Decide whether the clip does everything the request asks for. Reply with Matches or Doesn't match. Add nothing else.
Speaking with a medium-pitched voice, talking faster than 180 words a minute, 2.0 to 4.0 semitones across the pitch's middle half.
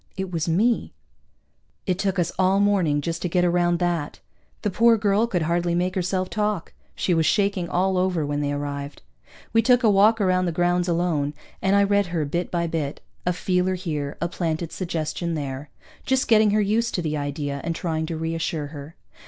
Matches